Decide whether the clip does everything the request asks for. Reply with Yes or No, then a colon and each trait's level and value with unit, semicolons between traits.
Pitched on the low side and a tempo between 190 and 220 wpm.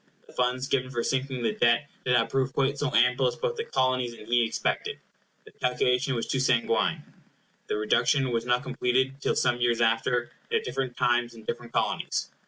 Yes: low, 125 Hz; average, 195 wpm